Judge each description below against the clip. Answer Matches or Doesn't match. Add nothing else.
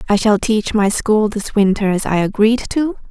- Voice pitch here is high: Matches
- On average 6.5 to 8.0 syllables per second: Doesn't match